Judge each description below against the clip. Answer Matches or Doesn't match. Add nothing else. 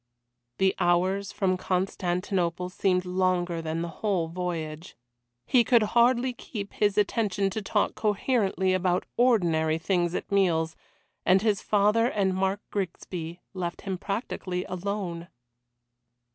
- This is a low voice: Doesn't match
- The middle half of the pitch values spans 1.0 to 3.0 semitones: Matches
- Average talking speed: Doesn't match